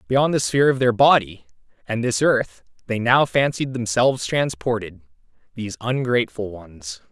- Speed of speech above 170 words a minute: No, average, 145 wpm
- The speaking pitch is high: No, low, 115 Hz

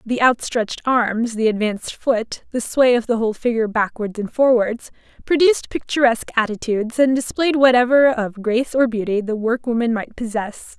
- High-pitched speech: Yes, high, 235 Hz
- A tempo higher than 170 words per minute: No, average, 165 wpm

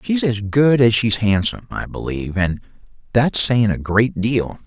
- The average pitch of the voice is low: Yes, low, 110 Hz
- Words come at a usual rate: Yes, average, 180 wpm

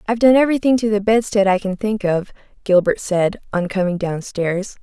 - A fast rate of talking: No, average, 185 wpm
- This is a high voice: Yes, high, 205 Hz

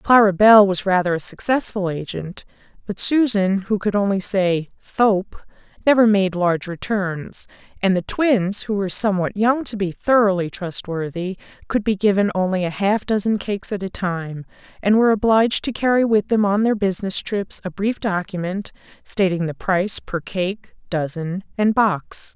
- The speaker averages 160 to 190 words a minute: Yes, average, 165 wpm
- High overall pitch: Yes, high, 195 Hz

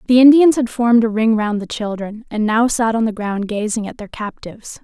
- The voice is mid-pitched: No, high, 225 Hz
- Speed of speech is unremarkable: No, fast, 235 wpm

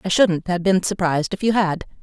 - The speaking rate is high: Yes, fast, 235 wpm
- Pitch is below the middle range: No, medium, 185 Hz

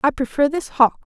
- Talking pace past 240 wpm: No, average, 200 wpm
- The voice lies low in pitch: No, very high, 280 Hz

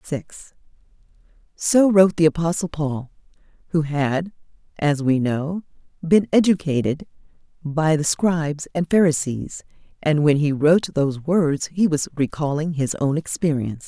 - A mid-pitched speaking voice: Yes, medium, 155 Hz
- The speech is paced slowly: Yes, slow, 130 wpm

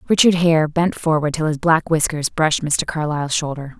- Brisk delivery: No, average, 190 wpm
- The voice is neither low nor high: Yes, medium, 155 Hz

